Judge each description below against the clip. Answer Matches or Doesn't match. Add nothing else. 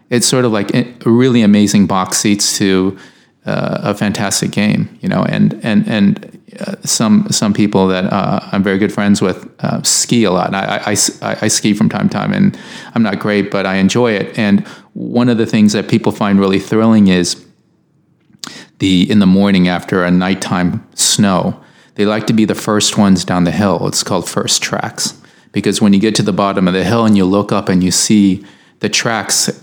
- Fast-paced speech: Matches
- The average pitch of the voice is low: Matches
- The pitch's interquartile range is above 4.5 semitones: Doesn't match